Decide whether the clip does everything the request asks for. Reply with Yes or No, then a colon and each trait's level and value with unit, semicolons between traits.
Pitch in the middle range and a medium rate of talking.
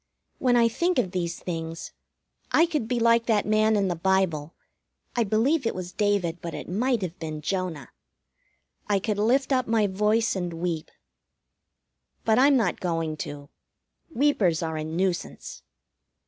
No: high, 195 Hz; average, 160 wpm